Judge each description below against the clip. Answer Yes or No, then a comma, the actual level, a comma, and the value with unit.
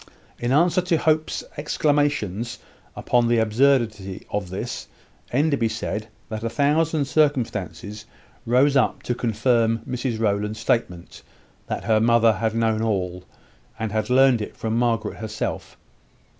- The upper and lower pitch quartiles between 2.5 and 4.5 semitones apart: Yes, average, 3.9 semitones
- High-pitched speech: No, low, 115 Hz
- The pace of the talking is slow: Yes, slow, 130 wpm